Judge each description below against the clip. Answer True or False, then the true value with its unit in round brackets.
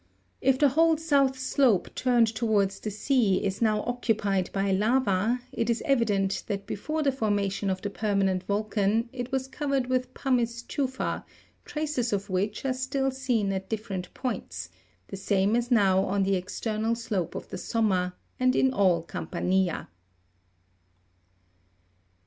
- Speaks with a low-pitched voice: False (220 Hz)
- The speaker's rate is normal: True (150 wpm)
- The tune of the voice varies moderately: True (4.6 semitones)